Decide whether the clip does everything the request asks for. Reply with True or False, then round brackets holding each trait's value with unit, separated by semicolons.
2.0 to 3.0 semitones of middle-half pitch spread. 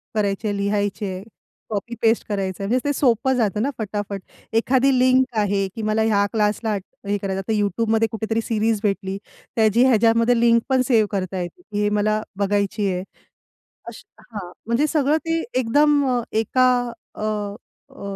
True (2.7 semitones)